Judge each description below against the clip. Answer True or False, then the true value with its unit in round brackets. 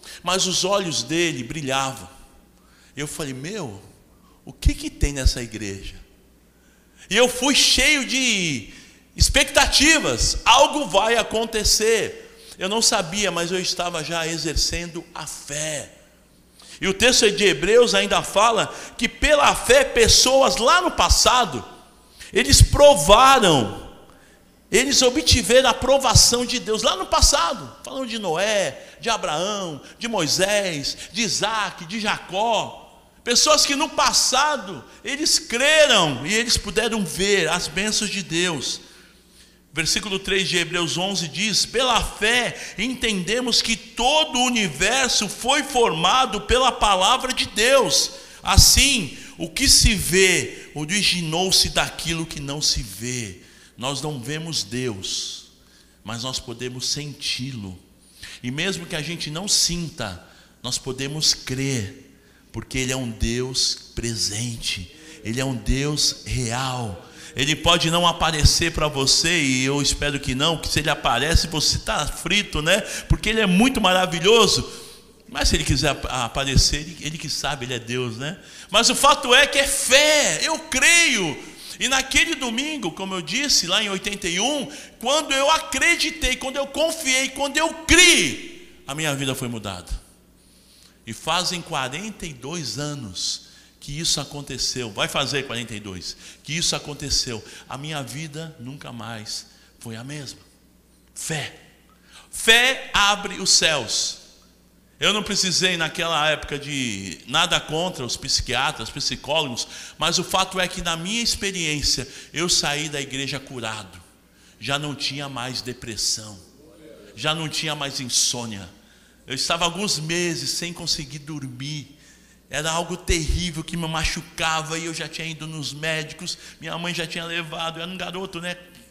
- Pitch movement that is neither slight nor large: False (8.1 semitones)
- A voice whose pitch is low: False (165 Hz)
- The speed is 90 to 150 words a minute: True (140 wpm)